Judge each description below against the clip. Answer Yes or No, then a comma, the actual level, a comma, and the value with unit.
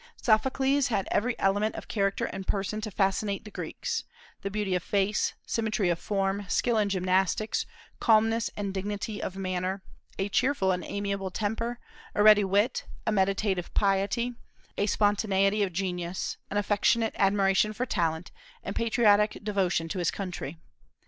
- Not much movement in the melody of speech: Yes, narrow, 2.0 semitones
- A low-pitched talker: No, high, 200 Hz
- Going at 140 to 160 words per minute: Yes, average, 150 wpm